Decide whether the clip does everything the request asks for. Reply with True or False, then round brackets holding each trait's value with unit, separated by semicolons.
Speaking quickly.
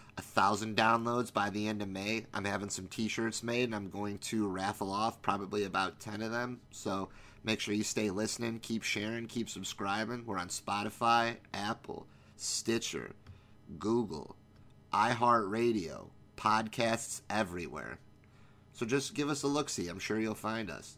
False (160 wpm)